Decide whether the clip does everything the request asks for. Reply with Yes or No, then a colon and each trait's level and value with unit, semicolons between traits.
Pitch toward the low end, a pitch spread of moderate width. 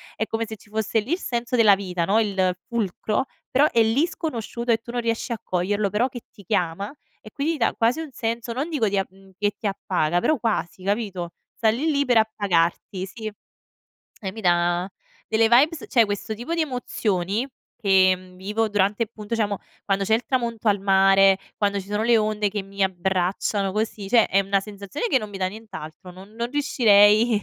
No: high, 210 Hz; average, 3.1 semitones